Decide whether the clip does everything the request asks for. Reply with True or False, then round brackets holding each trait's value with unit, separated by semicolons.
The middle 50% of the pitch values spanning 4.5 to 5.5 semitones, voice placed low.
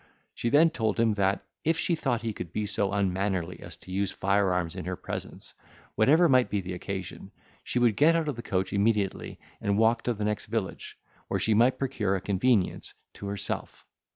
False (3.8 semitones; 105 Hz)